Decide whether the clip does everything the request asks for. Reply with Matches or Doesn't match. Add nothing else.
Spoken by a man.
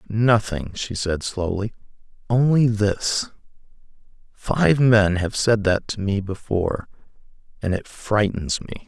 Matches